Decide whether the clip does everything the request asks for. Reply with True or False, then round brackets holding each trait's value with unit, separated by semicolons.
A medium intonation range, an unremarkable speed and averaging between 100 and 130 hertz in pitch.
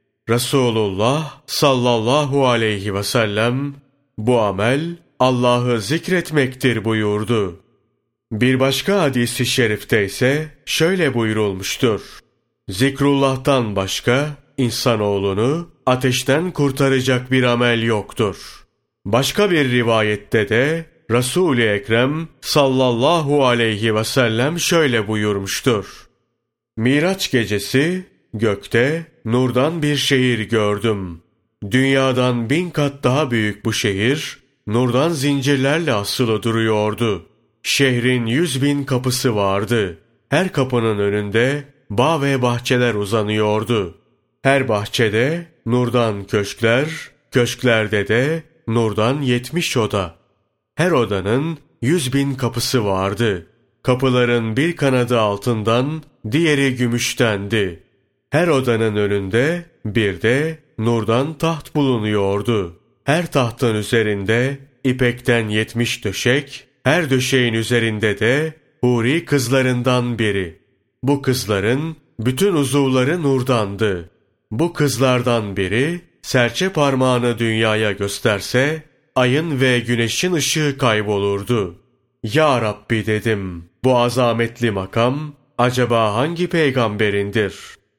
False (3.9 semitones; 90 wpm; 125 Hz)